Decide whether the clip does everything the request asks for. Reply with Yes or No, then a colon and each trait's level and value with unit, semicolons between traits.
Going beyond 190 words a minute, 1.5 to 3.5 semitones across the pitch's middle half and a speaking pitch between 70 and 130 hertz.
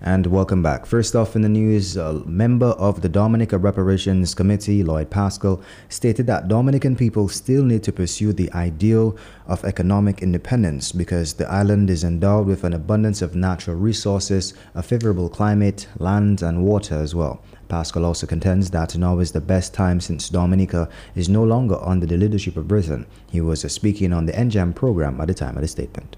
No: average, 185 wpm; average, 3.2 semitones; very low, 95 Hz